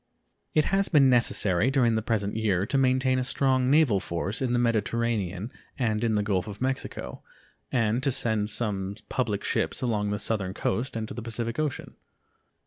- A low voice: Yes, low, 115 Hz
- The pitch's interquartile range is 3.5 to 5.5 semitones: Yes, average, 3.8 semitones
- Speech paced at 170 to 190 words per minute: Yes, average, 180 wpm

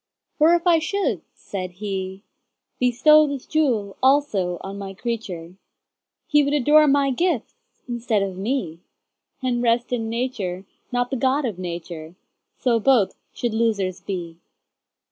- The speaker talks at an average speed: No, slow, 125 wpm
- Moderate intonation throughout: No, wide, 6.1 semitones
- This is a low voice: No, high, 230 Hz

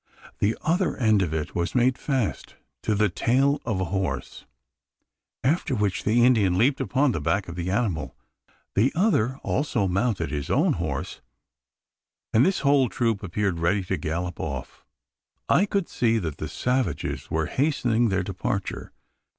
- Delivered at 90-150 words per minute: No, average, 160 wpm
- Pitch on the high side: No, low, 105 Hz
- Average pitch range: No, wide, 6.1 semitones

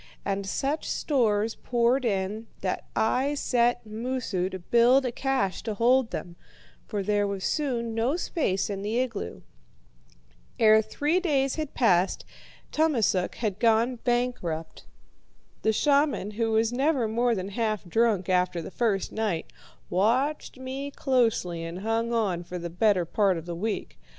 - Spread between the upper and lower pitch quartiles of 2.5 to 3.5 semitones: No, average, 4.6 semitones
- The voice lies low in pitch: No, high, 225 Hz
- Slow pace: No, average, 150 wpm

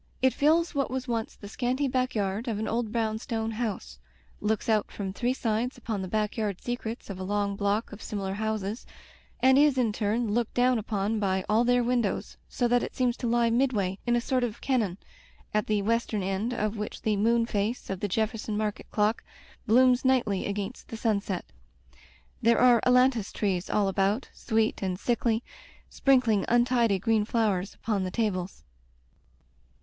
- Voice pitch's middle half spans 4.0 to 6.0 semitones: No, average, 3.0 semitones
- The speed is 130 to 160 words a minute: No, average, 175 wpm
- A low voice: No, high, 220 Hz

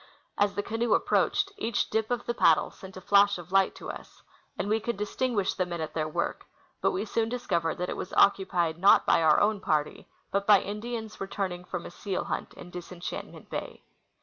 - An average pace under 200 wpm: No, fast, 205 wpm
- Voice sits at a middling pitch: No, high, 195 Hz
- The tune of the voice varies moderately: Yes, average, 3.5 semitones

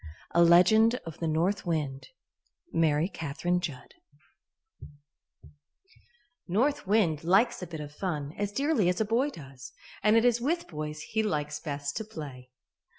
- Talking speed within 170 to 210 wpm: No, average, 150 wpm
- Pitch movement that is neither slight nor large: No, wide, 6.4 semitones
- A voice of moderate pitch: Yes, medium, 170 Hz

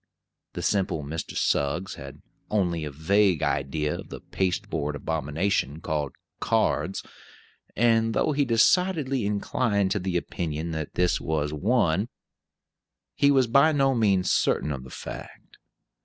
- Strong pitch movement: Yes, wide, 6.7 semitones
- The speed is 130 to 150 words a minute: Yes, slow, 135 wpm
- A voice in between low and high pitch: No, very low, 90 Hz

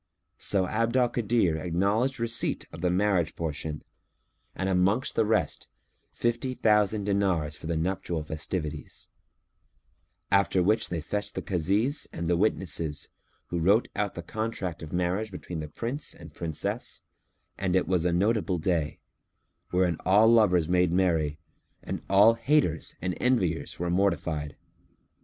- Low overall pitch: Yes, very low, 90 Hz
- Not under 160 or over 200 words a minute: No, average, 145 wpm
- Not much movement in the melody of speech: No, average, 4.3 semitones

